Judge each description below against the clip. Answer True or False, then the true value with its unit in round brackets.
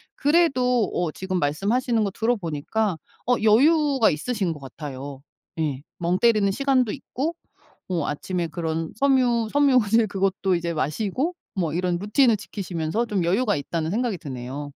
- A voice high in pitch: True (195 Hz)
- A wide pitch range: True (6.8 semitones)